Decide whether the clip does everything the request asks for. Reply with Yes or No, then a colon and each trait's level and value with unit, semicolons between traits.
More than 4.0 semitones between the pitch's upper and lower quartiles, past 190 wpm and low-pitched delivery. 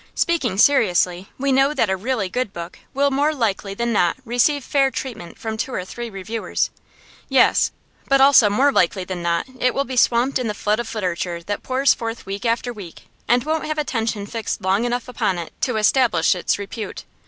No: average, 5.2 semitones; average, 200 wpm; high, 230 Hz